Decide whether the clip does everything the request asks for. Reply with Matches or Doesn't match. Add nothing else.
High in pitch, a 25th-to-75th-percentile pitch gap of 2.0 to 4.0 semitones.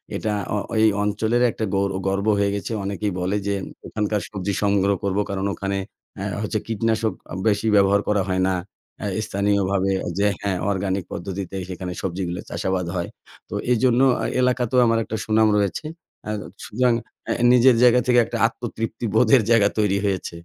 Doesn't match